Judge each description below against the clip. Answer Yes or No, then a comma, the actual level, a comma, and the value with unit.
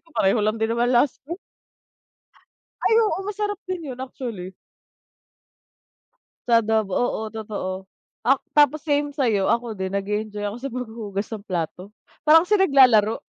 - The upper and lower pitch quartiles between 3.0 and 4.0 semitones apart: No, wide, 5.5 semitones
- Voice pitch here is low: No, high, 230 Hz